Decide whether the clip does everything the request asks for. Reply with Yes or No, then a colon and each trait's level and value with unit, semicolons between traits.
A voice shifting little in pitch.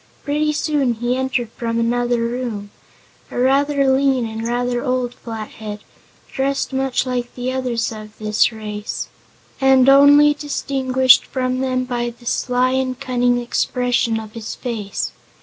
Yes: narrow, 2.2 semitones